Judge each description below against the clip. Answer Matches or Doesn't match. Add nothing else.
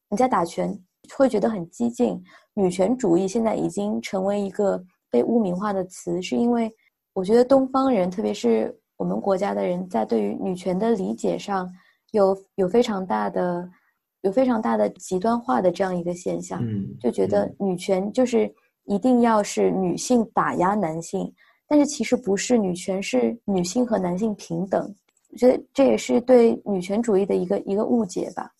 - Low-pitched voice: Doesn't match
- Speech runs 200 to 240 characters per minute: Doesn't match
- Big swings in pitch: Doesn't match